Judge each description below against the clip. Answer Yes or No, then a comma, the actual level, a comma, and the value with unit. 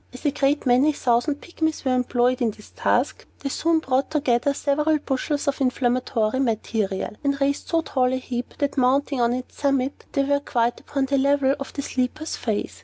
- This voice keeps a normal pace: Yes, average, 190 wpm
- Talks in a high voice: Yes, very high, 270 Hz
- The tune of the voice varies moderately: No, narrow, 2.3 semitones